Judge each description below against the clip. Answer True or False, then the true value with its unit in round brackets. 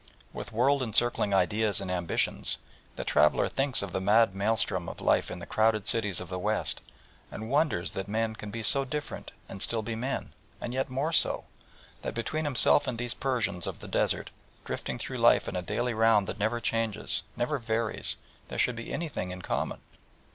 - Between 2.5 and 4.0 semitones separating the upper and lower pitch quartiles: True (3.7 semitones)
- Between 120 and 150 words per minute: False (190 wpm)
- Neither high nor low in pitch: False (110 Hz)